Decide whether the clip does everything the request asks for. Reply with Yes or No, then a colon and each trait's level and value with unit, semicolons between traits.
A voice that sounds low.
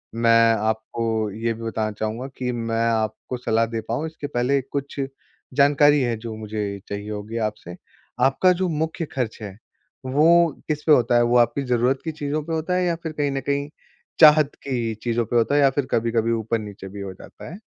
Yes: low, 120 Hz